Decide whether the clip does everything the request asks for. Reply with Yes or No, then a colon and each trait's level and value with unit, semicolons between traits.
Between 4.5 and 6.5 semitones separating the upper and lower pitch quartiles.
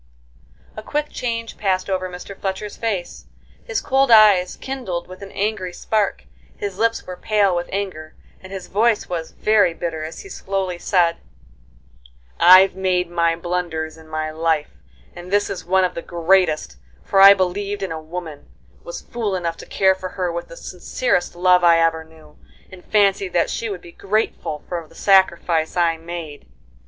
No: average, 2.9 semitones